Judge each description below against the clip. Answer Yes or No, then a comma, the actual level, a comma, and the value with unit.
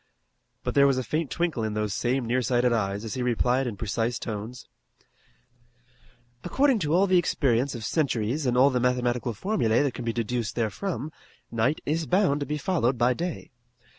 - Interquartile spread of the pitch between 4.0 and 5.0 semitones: Yes, average, 4.3 semitones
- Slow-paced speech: No, average, 180 wpm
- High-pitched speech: No, low, 125 Hz